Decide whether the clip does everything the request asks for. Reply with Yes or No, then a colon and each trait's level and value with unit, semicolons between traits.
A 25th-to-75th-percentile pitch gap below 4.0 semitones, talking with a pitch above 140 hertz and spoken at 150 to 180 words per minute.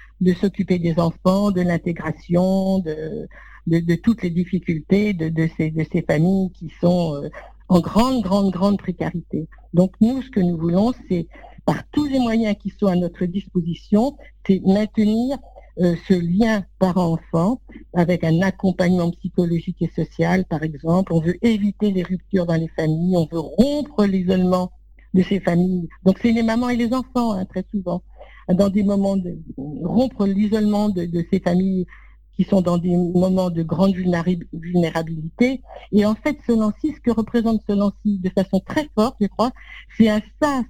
Yes: average, 3.4 semitones; high, 190 Hz; average, 175 wpm